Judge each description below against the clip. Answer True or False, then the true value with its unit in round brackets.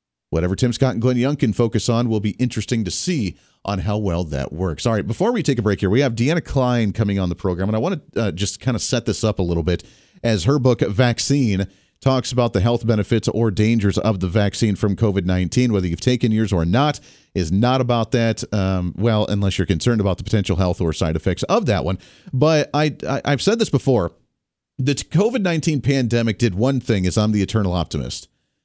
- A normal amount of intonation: True (4.7 semitones)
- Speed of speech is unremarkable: False (225 wpm)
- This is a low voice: True (110 Hz)